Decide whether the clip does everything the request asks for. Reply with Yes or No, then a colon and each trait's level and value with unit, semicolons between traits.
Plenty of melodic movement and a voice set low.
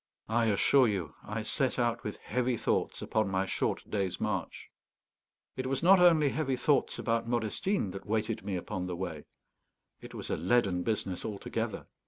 No: average, 4.8 semitones; low, 110 Hz